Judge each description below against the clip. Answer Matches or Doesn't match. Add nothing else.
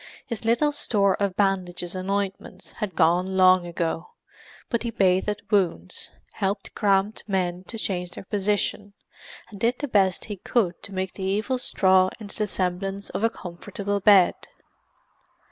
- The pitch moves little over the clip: Matches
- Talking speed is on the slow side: Doesn't match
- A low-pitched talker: Doesn't match